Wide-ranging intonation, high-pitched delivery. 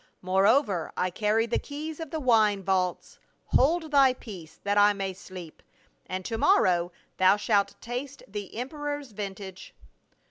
Yes: wide, 5.9 semitones; high, 210 Hz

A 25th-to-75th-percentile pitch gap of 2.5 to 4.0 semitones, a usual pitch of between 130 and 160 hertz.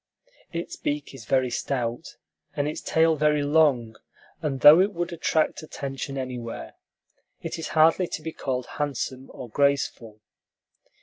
Yes: average, 3.6 semitones; medium, 140 Hz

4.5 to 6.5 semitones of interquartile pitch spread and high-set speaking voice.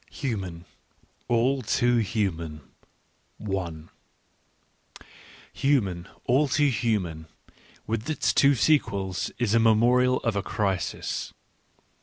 No: average, 4.9 semitones; low, 115 Hz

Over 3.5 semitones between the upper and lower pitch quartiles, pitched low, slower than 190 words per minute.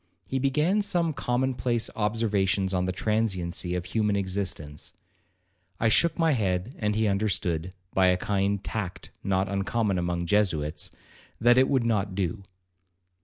Yes: average, 4.0 semitones; low, 100 Hz; average, 150 wpm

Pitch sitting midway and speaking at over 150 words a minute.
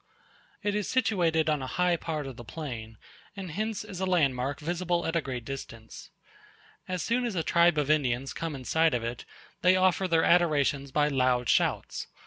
Yes: medium, 160 Hz; average, 190 wpm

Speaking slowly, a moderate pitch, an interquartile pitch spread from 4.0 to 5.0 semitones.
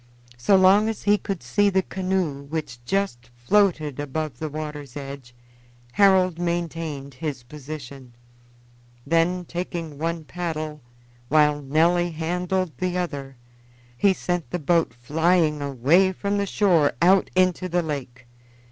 Yes: slow, 130 wpm; medium, 160 Hz; average, 4.3 semitones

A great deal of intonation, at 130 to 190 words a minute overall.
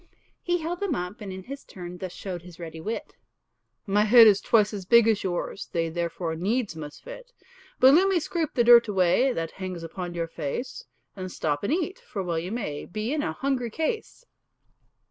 No: wide, 6.8 semitones; fast, 205 wpm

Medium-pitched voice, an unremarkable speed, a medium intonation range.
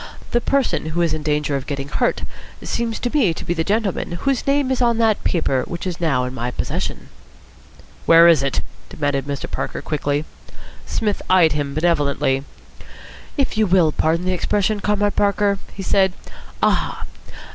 No: medium, 175 Hz; average, 170 wpm; wide, 6.0 semitones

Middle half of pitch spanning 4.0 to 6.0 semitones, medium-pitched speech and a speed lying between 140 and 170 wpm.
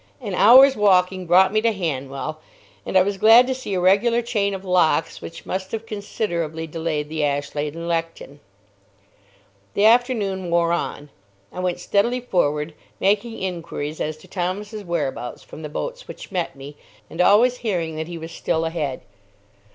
Yes: average, 4.5 semitones; medium, 180 Hz; average, 165 wpm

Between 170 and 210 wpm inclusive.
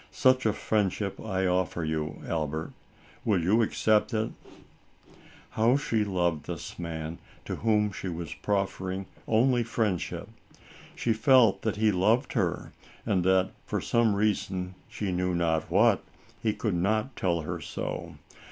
No: average, 145 wpm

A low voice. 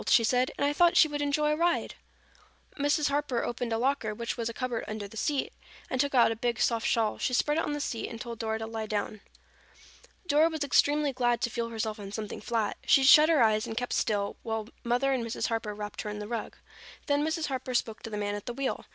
No: high, 240 Hz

